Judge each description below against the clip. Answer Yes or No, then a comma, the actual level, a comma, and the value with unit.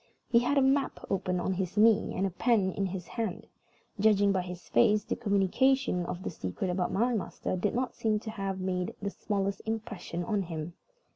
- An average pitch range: Yes, average, 3.4 semitones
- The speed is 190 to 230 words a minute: Yes, average, 200 wpm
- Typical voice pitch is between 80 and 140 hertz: No, high, 195 Hz